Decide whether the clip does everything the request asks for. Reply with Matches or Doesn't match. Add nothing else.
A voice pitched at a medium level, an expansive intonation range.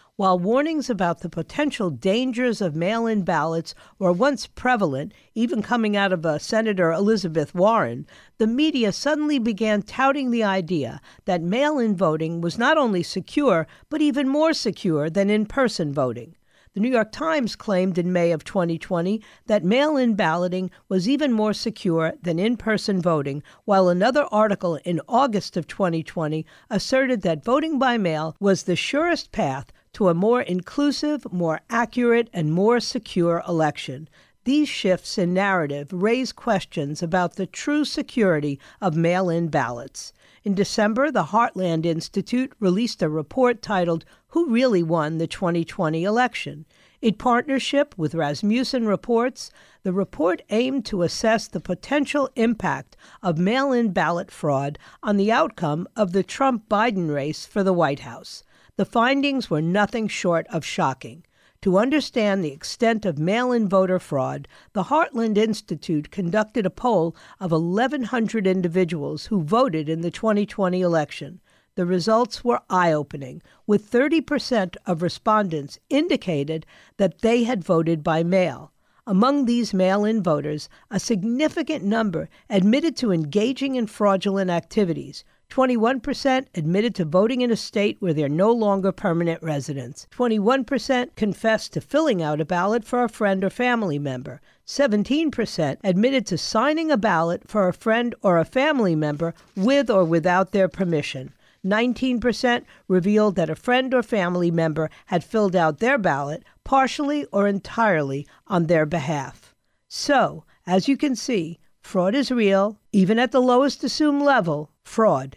Doesn't match